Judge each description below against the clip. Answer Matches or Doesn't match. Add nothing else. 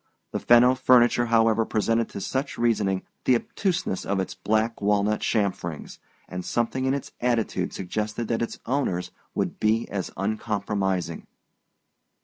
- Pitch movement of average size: Matches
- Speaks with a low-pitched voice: Matches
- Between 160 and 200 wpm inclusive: Doesn't match